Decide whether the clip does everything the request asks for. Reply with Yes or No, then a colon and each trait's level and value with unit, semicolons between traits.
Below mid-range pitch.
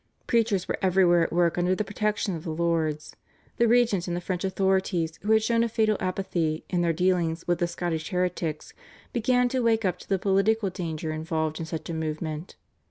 No: medium, 180 Hz